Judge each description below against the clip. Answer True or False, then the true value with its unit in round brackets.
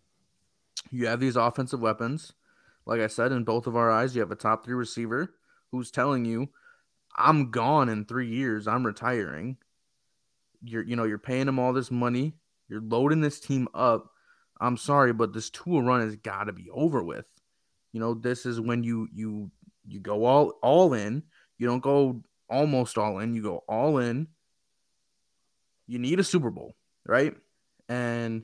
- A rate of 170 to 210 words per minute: True (175 wpm)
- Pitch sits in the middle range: False (120 Hz)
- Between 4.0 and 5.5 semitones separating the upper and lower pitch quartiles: False (2.5 semitones)